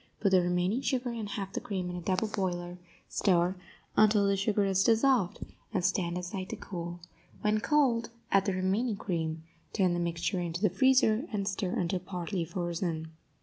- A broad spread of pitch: No, average, 3.2 semitones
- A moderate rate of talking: Yes, average, 180 wpm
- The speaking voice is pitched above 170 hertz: Yes, high, 190 Hz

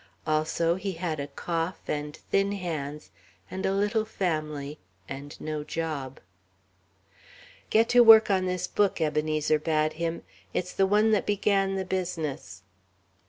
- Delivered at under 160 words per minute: Yes, average, 140 wpm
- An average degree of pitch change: Yes, average, 4.2 semitones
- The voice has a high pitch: No, medium, 165 Hz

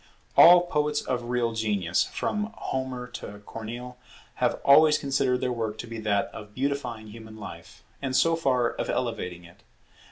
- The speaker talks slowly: No, average, 160 wpm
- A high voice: No, low, 125 Hz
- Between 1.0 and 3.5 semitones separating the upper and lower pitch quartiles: No, average, 4.0 semitones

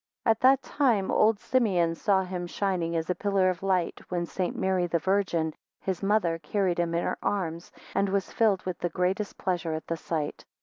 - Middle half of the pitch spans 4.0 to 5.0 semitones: No, average, 2.7 semitones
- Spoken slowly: No, fast, 205 wpm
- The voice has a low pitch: No, medium, 185 Hz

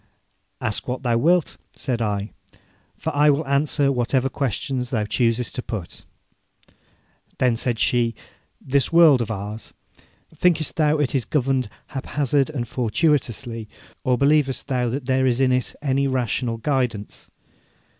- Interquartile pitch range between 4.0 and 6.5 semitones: No, average, 3.0 semitones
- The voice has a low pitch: Yes, low, 130 Hz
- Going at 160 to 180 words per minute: No, average, 140 wpm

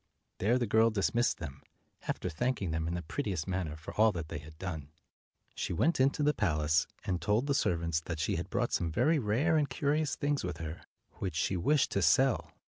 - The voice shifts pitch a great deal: Yes, wide, 7.8 semitones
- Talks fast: Yes, fast, 210 wpm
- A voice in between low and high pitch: No, very low, 95 Hz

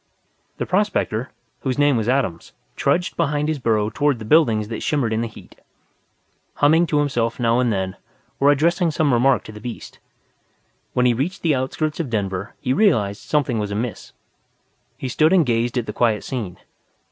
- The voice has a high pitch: No, low, 125 Hz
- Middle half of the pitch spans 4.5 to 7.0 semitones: Yes, average, 5.0 semitones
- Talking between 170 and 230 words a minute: Yes, average, 180 wpm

